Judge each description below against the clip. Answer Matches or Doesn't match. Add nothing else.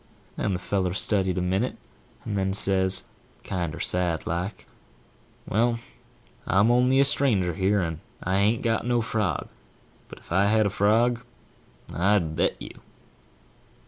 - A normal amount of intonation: Matches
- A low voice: Matches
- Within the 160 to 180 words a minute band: Doesn't match